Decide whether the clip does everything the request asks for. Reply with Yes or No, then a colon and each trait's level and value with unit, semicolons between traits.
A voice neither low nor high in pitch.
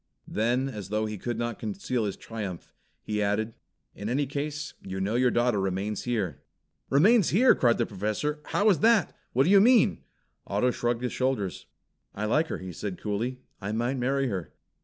No: low, 120 Hz